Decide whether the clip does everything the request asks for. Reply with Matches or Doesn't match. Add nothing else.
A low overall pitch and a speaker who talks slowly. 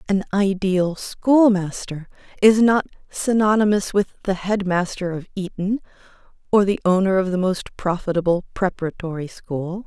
Doesn't match